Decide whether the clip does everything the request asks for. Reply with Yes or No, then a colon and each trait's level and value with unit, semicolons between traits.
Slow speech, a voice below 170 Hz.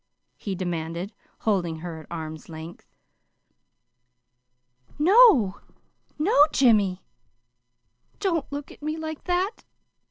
No: slow, 95 wpm; high, 210 Hz